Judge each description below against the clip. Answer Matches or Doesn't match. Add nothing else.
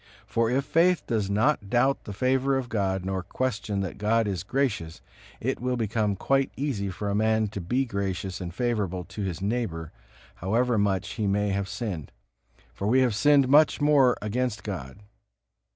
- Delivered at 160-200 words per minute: Matches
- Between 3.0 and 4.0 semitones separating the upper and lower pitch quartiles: Doesn't match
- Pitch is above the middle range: Doesn't match